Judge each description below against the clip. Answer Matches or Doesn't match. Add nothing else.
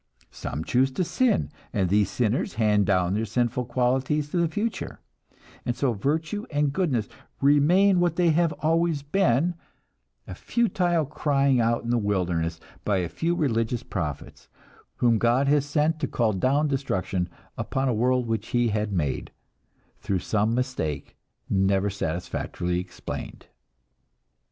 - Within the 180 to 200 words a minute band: Doesn't match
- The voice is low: Matches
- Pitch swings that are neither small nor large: Doesn't match